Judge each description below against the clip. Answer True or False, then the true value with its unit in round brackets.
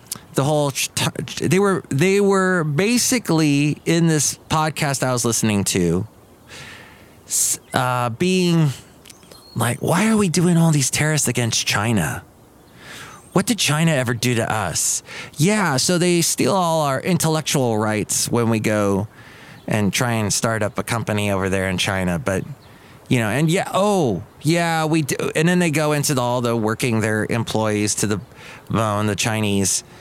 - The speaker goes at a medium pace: True (160 wpm)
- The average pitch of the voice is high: False (130 Hz)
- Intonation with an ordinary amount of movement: False (6.8 semitones)